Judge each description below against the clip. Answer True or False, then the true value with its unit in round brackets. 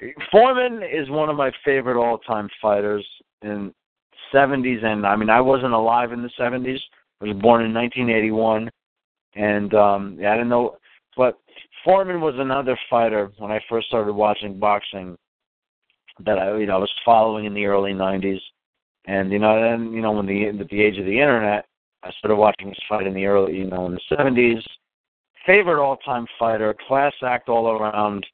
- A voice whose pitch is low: True (110 Hz)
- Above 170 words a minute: True (180 wpm)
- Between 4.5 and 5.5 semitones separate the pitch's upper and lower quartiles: False (2.9 semitones)